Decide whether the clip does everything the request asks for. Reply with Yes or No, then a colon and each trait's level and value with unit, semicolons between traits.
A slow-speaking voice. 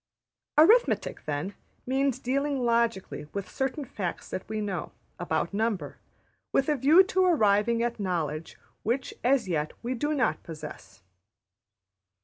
Yes: slow, 130 wpm